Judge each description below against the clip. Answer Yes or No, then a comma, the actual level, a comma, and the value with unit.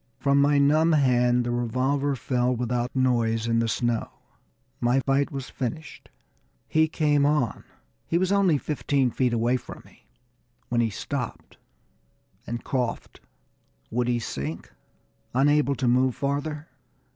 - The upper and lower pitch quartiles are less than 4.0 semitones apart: Yes, average, 3.1 semitones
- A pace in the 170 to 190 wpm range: No, slow, 135 wpm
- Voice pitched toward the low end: Yes, low, 130 Hz